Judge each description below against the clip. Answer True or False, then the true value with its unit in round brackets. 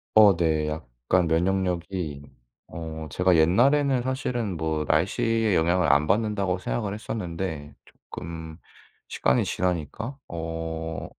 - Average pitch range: True (4.2 semitones)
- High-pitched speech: False (85 Hz)